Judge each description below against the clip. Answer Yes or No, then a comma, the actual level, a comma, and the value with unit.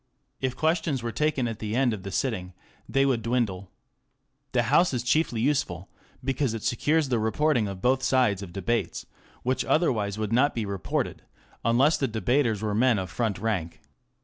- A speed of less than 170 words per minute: No, average, 175 wpm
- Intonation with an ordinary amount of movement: Yes, average, 4.2 semitones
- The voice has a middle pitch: No, low, 120 Hz